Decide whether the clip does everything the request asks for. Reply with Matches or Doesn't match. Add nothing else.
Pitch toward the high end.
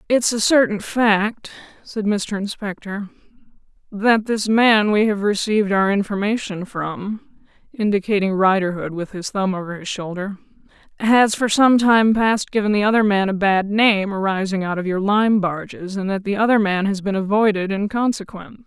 Matches